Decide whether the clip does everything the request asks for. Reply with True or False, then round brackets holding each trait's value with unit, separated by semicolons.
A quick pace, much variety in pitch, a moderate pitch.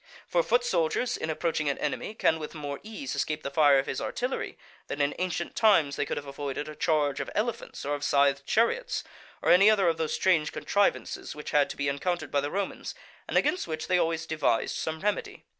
True (215 wpm; 5.8 semitones; 160 Hz)